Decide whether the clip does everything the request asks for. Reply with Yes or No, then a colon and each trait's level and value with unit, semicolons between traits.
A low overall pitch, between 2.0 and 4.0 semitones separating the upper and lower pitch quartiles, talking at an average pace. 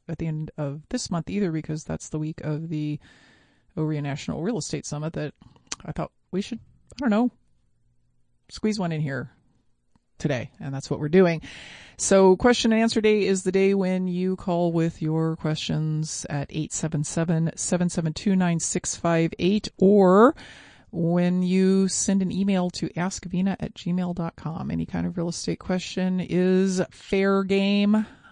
No: medium, 175 Hz; average, 3.7 semitones; average, 155 wpm